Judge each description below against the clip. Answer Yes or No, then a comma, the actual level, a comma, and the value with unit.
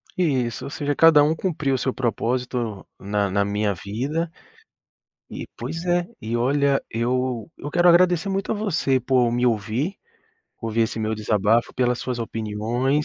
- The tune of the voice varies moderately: Yes, average, 5.0 semitones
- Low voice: Yes, low, 125 Hz